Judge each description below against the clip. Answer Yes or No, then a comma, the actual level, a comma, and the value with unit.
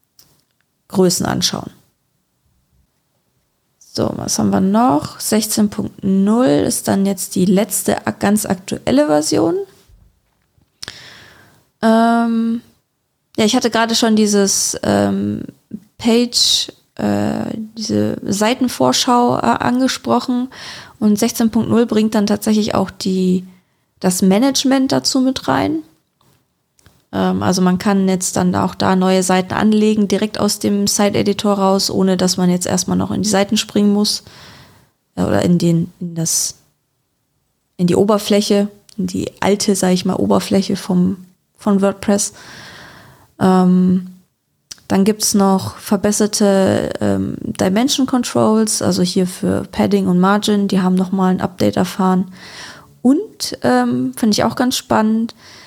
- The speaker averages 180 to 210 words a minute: No, slow, 125 wpm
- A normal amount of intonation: Yes, average, 3.0 semitones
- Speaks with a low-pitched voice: No, high, 200 Hz